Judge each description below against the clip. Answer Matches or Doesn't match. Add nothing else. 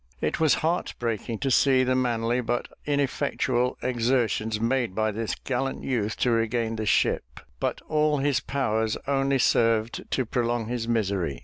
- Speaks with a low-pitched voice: Matches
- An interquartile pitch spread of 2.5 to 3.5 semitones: Matches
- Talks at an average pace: Matches